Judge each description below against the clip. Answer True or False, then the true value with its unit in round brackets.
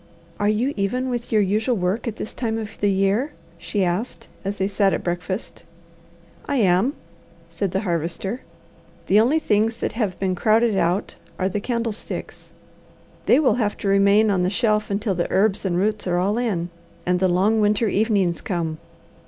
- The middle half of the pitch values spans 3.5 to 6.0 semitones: False (3.0 semitones)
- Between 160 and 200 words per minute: True (180 wpm)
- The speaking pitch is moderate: False (205 Hz)